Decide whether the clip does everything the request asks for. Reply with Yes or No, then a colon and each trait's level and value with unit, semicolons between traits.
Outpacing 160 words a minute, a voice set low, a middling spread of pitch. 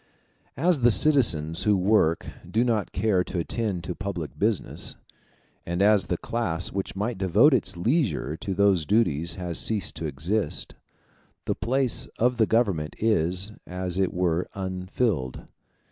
No: average, 145 wpm; very low, 95 Hz; average, 4.4 semitones